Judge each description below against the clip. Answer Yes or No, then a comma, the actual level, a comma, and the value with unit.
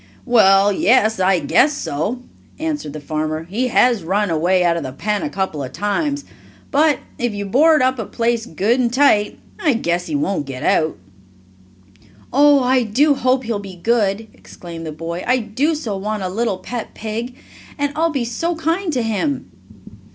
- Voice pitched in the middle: No, high, 225 Hz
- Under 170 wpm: No, average, 180 wpm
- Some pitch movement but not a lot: No, wide, 5.7 semitones